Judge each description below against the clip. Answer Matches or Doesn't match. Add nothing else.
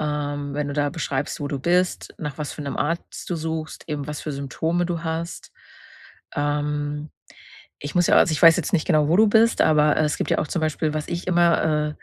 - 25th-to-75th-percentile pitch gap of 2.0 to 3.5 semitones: Matches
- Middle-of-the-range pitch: Matches